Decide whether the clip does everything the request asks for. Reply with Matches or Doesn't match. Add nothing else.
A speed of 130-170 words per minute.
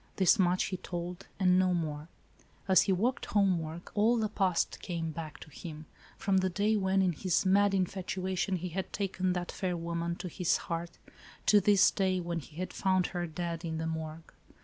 Doesn't match